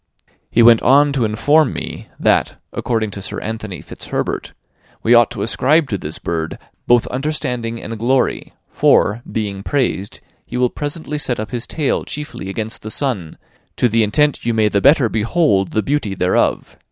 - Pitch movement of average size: Yes, average, 4.5 semitones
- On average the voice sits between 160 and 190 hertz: No, low, 115 Hz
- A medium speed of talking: Yes, average, 170 wpm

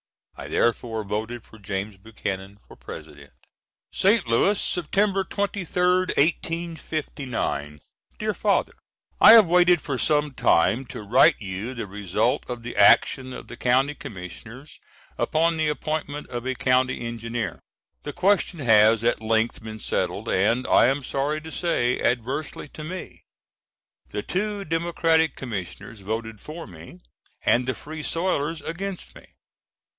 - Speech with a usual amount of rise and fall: No, wide, 6.6 semitones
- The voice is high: No, low, 130 Hz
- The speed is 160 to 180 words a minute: No, average, 140 wpm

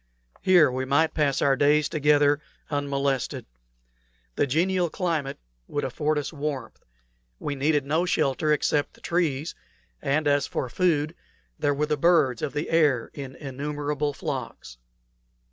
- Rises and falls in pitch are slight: Yes, narrow, 2.0 semitones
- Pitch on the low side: No, medium, 145 Hz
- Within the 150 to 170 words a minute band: No, average, 140 wpm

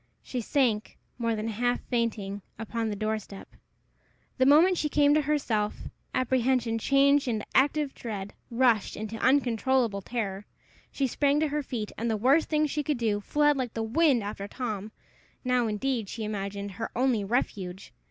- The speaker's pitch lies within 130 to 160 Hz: No, high, 235 Hz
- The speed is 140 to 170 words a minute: Yes, average, 165 wpm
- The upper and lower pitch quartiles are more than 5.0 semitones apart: No, average, 4.2 semitones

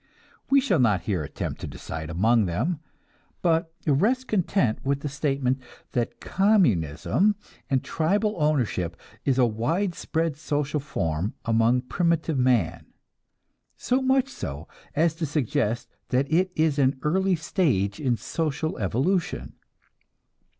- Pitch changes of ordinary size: No, wide, 6.7 semitones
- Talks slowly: Yes, slow, 125 wpm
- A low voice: No, medium, 145 Hz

